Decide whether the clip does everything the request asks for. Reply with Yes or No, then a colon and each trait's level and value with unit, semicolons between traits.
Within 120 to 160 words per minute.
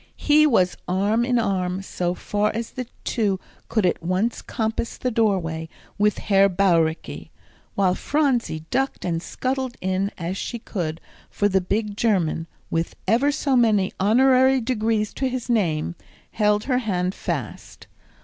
Yes: average, 150 wpm